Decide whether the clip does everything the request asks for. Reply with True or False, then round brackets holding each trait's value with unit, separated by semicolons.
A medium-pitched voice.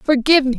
False (280 Hz)